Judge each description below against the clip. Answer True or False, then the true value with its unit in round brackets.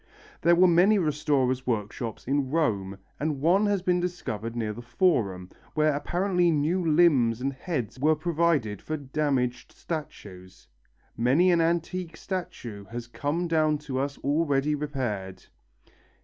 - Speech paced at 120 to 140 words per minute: True (135 wpm)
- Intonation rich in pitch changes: True (5.8 semitones)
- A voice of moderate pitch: True (145 Hz)